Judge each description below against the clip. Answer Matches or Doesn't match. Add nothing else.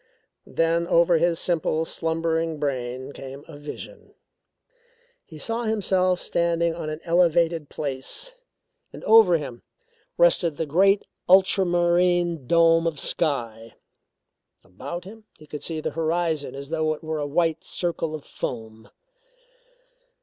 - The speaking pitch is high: Doesn't match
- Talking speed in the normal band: Doesn't match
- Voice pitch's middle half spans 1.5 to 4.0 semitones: Matches